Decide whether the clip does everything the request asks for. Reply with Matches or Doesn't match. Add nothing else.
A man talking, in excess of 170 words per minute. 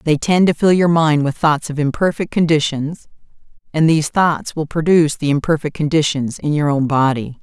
Doesn't match